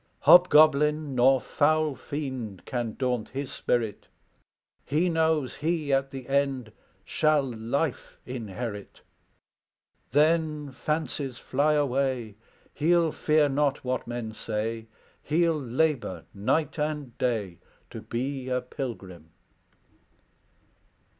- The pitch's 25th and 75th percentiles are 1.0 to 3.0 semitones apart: No, average, 4.0 semitones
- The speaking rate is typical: No, slow, 100 wpm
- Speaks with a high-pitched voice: No, low, 135 Hz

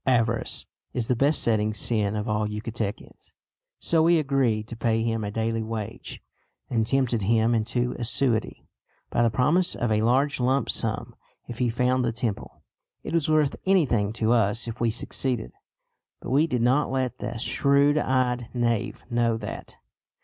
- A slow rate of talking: No, average, 165 wpm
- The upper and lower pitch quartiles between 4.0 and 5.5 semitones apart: No, average, 2.8 semitones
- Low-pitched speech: Yes, low, 120 Hz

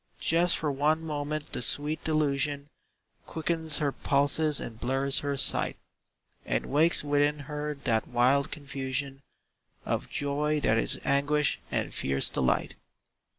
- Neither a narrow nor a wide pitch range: No, narrow, 1.7 semitones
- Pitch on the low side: No, medium, 145 Hz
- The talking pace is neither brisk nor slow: No, slow, 130 wpm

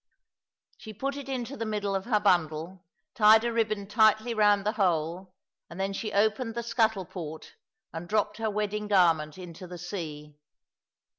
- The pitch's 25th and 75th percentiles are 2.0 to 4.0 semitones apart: Yes, average, 3.7 semitones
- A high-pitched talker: Yes, high, 205 Hz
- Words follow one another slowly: No, average, 165 wpm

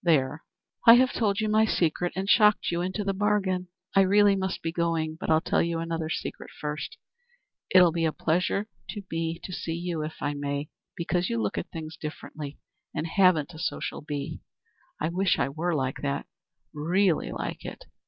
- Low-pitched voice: No, medium, 170 Hz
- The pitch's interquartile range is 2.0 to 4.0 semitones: Yes, average, 3.5 semitones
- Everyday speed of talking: Yes, average, 190 wpm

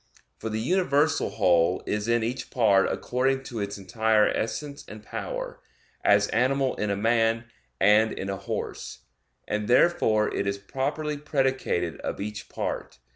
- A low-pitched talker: Yes, low, 110 Hz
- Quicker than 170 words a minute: No, average, 150 wpm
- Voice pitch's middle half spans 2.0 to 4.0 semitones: No, average, 4.5 semitones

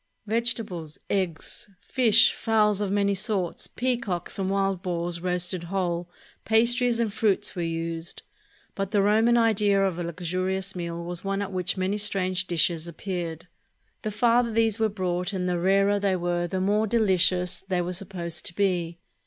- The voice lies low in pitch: No, high, 190 Hz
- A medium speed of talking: Yes, average, 160 wpm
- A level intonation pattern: No, average, 3.0 semitones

